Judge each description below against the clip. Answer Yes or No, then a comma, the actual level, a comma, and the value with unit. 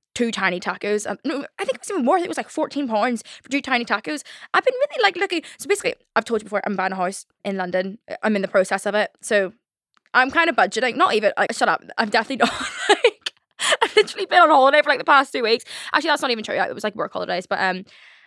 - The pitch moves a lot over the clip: Yes, wide, 7.3 semitones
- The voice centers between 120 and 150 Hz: No, very high, 250 Hz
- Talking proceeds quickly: Yes, fast, 275 wpm